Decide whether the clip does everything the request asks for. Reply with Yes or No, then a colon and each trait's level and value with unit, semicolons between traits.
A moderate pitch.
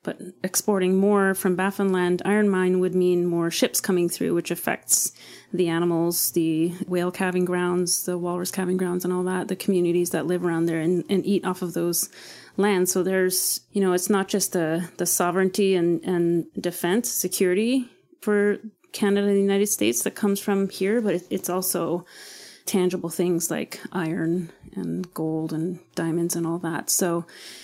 Yes: medium, 180 Hz